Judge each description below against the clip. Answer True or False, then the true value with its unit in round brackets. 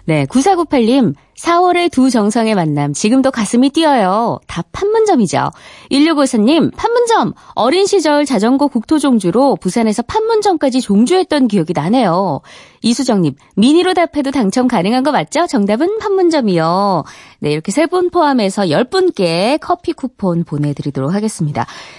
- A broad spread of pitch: True (8.3 semitones)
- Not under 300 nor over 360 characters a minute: True (310 characters per minute)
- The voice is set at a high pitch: True (255 Hz)